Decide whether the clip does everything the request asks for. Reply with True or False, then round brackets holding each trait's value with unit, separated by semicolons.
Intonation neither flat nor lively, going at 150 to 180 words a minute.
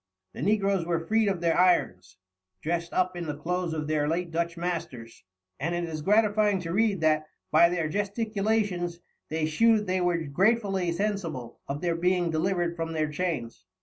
True (3.5 semitones; 175 wpm)